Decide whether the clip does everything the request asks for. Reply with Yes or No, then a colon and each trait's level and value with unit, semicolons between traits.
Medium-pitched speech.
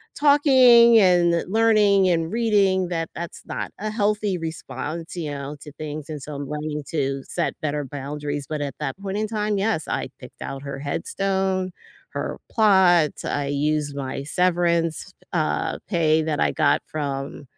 Yes: medium, 165 Hz